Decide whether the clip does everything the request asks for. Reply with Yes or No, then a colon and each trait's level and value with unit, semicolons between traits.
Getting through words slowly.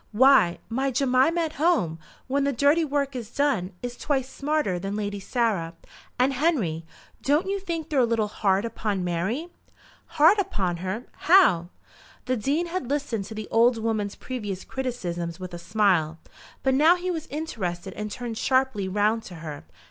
No: average, 170 wpm